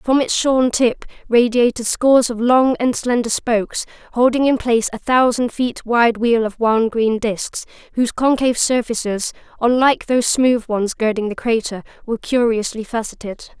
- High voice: Yes, high, 235 Hz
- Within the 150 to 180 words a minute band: Yes, average, 160 wpm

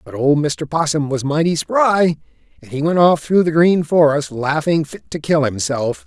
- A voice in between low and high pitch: Yes, medium, 150 Hz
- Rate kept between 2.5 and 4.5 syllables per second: Yes, 4.2 syllables/s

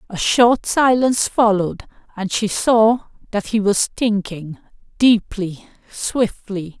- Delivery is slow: Yes, slow, 115 wpm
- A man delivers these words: No, female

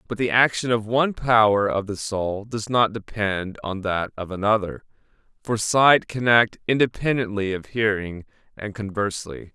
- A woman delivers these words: No, male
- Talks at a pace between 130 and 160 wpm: Yes, average, 155 wpm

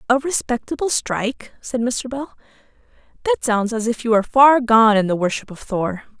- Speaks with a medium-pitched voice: No, high, 230 Hz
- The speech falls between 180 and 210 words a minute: Yes, average, 185 wpm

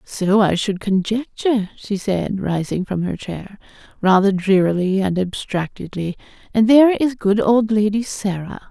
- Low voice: No, high, 205 Hz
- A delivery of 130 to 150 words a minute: Yes, average, 145 wpm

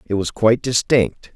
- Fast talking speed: No, average, 180 wpm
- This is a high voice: No, low, 110 Hz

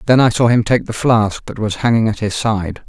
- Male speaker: Yes, male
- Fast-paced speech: Yes, fast, 270 wpm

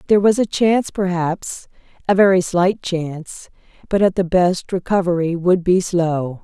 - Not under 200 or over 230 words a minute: No, average, 160 wpm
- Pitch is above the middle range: No, medium, 180 Hz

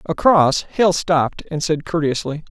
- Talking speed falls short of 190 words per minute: Yes, average, 140 wpm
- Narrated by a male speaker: Yes, male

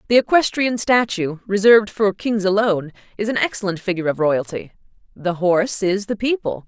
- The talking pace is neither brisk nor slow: Yes, average, 160 wpm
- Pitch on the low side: No, high, 200 Hz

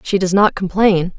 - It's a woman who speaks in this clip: Yes, female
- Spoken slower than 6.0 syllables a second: Yes, 4.7 syllables/s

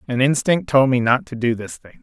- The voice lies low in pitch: Yes, low, 130 Hz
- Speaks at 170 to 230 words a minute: No, fast, 265 wpm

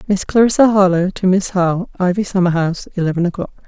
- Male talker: No, female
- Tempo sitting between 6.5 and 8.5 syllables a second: Yes, 6.7 syllables/s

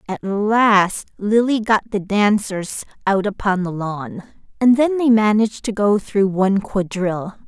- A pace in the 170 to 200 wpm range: No, average, 150 wpm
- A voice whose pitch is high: Yes, high, 205 Hz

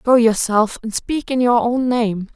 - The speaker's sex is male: No, female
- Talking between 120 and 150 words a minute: No, fast, 205 wpm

